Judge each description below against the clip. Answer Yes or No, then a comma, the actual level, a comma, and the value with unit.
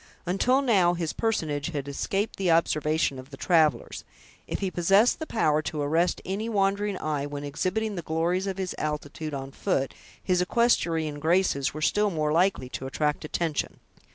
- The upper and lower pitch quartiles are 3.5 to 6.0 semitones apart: Yes, average, 4.5 semitones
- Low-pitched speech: No, medium, 165 Hz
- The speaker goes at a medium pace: Yes, average, 170 wpm